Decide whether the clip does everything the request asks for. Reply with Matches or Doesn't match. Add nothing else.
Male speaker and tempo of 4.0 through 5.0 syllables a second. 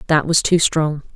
Doesn't match